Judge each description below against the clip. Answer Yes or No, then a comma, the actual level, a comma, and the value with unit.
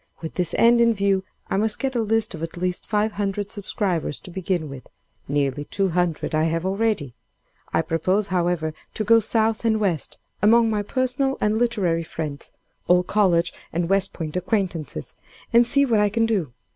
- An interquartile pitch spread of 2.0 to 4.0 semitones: No, average, 4.8 semitones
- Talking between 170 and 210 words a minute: Yes, average, 175 wpm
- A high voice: Yes, high, 195 Hz